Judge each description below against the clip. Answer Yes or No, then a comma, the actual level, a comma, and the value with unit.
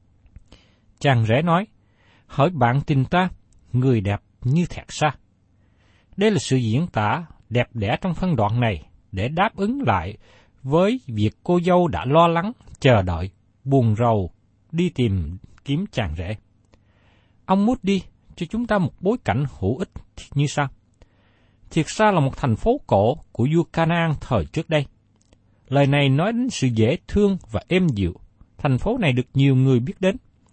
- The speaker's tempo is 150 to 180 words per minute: Yes, average, 170 wpm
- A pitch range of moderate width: No, wide, 8.2 semitones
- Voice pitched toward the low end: Yes, low, 125 Hz